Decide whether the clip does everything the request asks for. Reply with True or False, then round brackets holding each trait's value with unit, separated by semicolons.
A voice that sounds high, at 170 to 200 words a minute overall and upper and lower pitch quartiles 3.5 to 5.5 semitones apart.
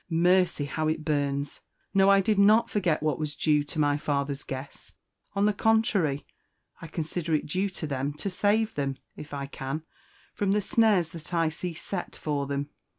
False (155 Hz; 185 wpm; 5.1 semitones)